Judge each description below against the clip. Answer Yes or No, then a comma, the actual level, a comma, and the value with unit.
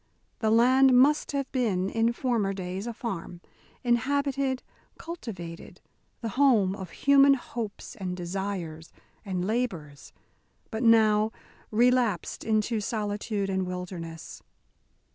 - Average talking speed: No, slow, 110 wpm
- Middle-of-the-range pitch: No, high, 215 Hz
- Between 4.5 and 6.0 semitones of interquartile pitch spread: Yes, average, 4.9 semitones